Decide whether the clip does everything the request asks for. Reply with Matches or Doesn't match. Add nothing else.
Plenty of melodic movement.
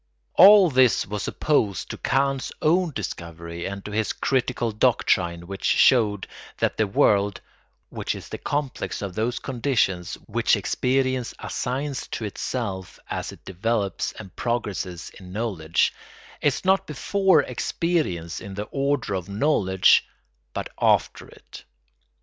Matches